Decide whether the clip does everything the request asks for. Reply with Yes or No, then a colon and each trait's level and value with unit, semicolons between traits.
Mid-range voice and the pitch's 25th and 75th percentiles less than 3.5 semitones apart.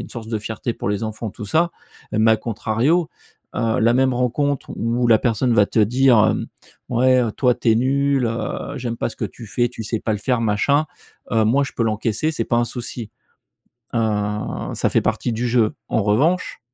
No: low, 120 Hz; narrow, 2.5 semitones